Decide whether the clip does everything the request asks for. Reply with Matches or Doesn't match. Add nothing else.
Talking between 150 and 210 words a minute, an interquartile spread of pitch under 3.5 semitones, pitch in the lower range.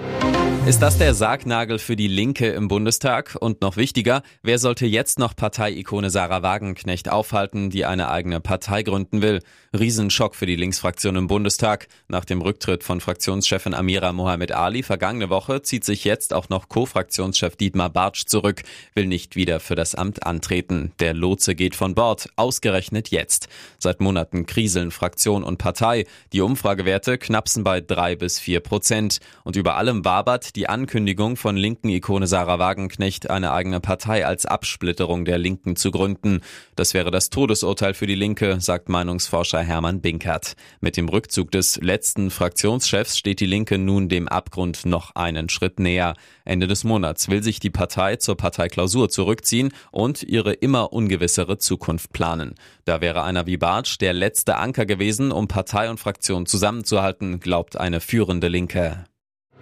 Matches